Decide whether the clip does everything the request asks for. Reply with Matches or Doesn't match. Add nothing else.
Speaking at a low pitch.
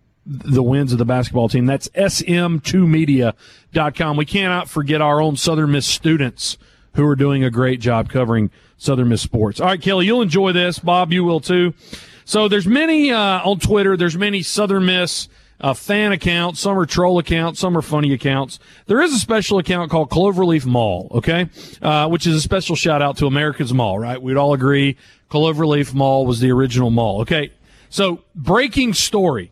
Doesn't match